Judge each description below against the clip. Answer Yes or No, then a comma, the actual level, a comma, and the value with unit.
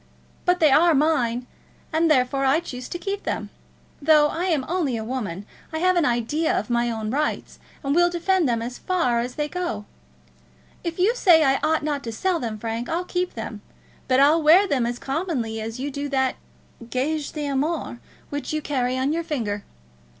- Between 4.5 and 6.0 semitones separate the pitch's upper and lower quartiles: Yes, average, 5.1 semitones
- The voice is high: Yes, very high, 285 Hz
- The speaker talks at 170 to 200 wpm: Yes, average, 195 wpm